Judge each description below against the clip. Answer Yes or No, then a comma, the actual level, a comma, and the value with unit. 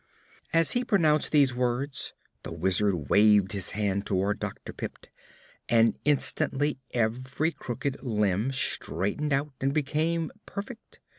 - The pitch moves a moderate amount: No, wide, 6.4 semitones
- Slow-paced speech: Yes, slow, 125 wpm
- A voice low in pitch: Yes, low, 130 Hz